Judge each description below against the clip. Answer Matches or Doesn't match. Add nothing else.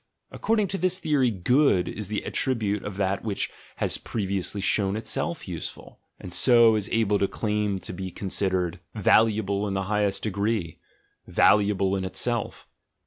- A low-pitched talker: Matches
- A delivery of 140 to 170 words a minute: Matches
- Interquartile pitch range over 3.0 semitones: Doesn't match